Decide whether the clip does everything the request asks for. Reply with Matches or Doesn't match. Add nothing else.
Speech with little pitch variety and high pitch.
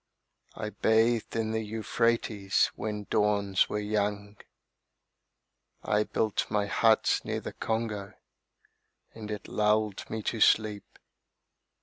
Doesn't match